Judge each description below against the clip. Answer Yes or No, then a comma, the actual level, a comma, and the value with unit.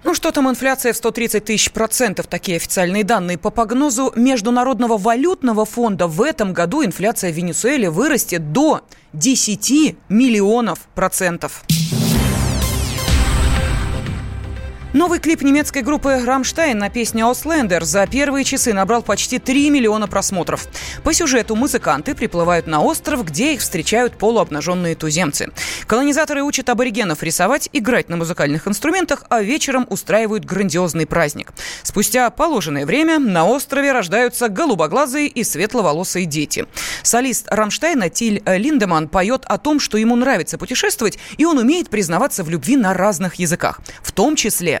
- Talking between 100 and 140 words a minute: Yes, average, 135 wpm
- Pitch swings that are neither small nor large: No, wide, 6.9 semitones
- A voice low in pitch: No, high, 225 Hz